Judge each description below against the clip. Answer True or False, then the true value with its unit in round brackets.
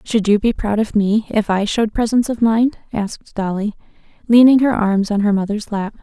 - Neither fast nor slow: False (210 wpm)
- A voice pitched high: True (215 Hz)